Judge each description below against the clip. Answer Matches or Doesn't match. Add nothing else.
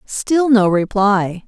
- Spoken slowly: Matches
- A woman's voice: Matches